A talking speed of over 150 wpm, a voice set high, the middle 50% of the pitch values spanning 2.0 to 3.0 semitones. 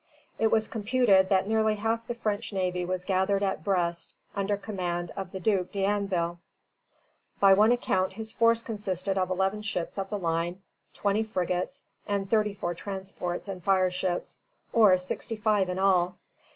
Yes: average, 160 wpm; high, 195 Hz; narrow, 2.6 semitones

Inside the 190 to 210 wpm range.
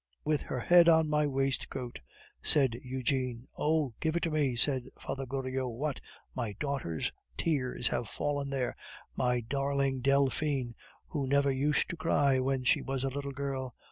No: average, 160 wpm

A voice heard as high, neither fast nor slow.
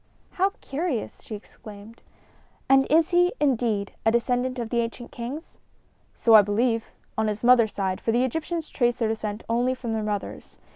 Yes: high, 235 Hz; average, 175 wpm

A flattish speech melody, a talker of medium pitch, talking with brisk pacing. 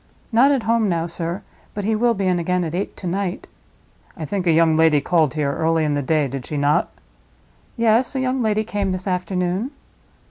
No: average, 4.8 semitones; medium, 180 Hz; fast, 210 wpm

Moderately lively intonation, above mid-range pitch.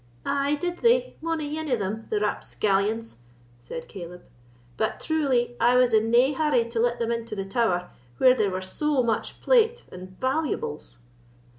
No: wide, 6.2 semitones; high, 240 Hz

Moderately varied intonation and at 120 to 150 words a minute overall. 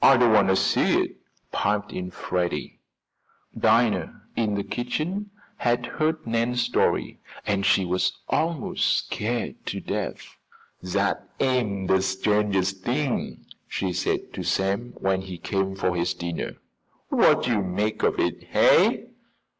Yes: average, 4.1 semitones; slow, 135 wpm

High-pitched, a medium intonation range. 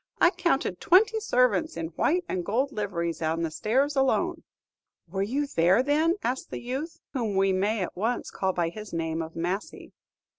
No: high, 215 Hz; wide, 8.1 semitones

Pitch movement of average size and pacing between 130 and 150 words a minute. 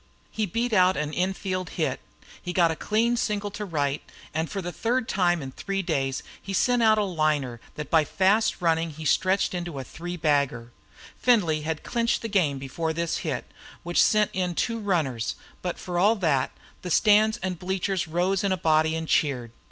No: average, 4.5 semitones; average, 200 wpm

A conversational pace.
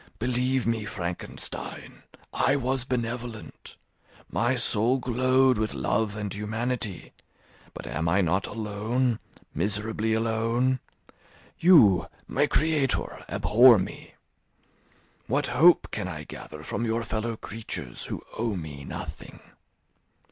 No: slow, 110 wpm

